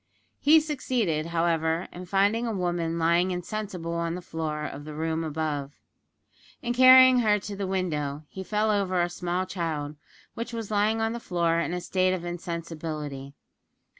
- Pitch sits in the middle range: Yes, medium, 175 Hz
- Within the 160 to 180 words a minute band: Yes, average, 165 wpm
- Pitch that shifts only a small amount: No, average, 4.3 semitones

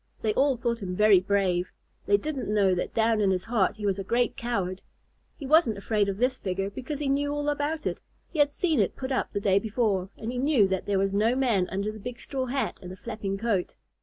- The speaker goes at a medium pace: No, fast, 245 wpm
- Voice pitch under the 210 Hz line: No, high, 220 Hz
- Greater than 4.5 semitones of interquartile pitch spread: Yes, average, 4.9 semitones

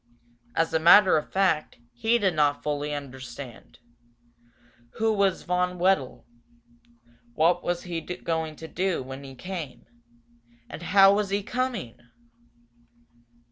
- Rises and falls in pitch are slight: No, average, 4.7 semitones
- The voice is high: No, medium, 175 Hz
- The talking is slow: Yes, slow, 125 wpm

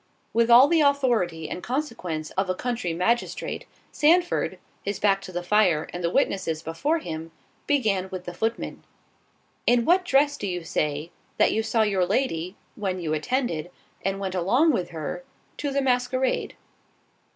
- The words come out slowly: No, average, 160 wpm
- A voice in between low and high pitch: No, high, 200 Hz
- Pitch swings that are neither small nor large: No, wide, 6.6 semitones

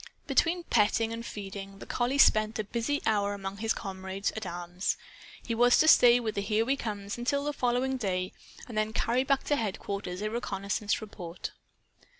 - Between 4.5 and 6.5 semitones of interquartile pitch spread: No, average, 3.5 semitones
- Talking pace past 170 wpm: Yes, average, 180 wpm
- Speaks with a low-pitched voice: No, high, 215 Hz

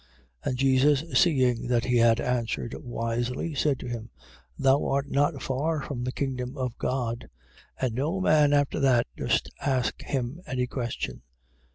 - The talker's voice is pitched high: No, low, 130 Hz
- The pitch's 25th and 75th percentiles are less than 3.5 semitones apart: Yes, average, 2.7 semitones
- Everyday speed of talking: Yes, average, 160 wpm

